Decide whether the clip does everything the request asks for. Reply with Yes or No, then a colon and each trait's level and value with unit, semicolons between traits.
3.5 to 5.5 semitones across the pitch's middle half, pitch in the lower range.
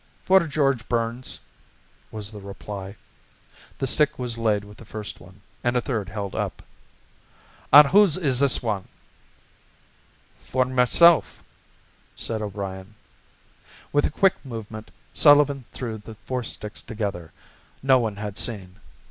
Yes: average, 4.6 semitones; low, 115 Hz